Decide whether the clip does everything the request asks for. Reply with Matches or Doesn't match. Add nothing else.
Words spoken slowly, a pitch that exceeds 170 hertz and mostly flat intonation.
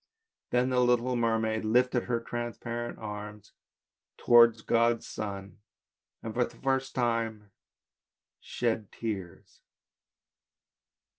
Doesn't match